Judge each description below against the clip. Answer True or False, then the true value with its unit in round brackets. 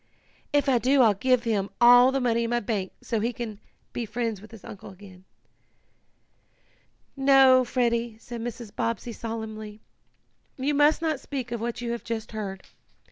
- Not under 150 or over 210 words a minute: True (170 wpm)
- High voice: True (235 Hz)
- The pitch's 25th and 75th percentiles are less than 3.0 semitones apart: True (2.6 semitones)